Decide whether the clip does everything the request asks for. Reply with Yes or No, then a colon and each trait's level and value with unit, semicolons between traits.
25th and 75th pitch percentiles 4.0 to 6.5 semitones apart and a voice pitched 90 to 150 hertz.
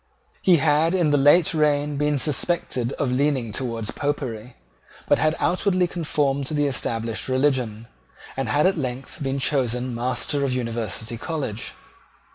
No: average, 3.5 semitones; medium, 140 Hz